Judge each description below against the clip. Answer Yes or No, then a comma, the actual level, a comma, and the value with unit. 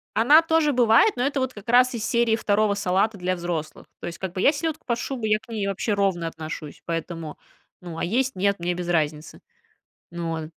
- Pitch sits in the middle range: No, high, 200 Hz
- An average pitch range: No, wide, 5.7 semitones